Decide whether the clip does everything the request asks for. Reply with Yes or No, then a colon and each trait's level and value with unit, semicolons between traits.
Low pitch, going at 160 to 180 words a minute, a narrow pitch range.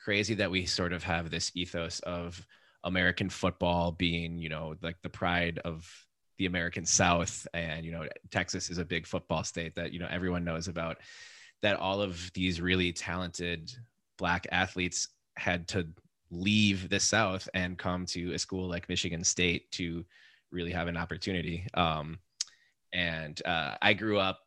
Yes: very low, 90 Hz; average, 165 wpm; narrow, 1.7 semitones